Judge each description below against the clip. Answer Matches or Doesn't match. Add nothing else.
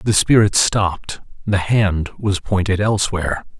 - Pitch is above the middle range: Doesn't match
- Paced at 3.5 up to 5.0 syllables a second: Matches